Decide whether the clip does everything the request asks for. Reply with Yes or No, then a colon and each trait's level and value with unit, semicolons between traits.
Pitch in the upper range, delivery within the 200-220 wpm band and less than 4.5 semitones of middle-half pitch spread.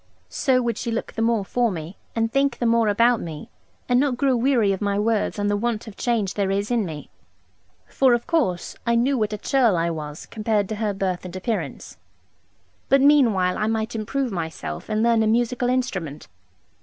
Yes: high, 220 Hz; fast, 205 wpm; average, 3.6 semitones